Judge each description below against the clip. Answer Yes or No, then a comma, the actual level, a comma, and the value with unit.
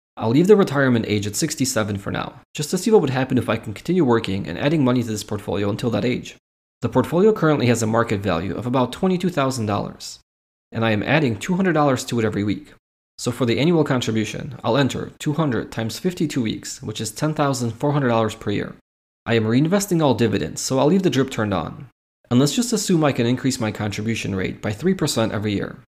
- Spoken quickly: Yes, fast, 210 wpm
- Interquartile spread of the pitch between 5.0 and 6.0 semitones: Yes, wide, 5.5 semitones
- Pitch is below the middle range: Yes, low, 125 Hz